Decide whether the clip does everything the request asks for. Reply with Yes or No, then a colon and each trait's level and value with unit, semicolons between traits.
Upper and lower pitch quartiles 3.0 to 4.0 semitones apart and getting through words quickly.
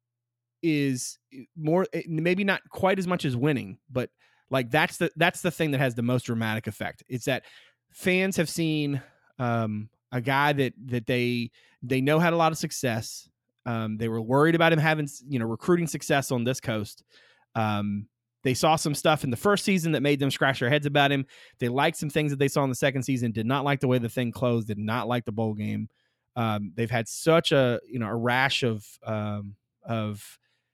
No: average, 4.7 semitones; fast, 210 wpm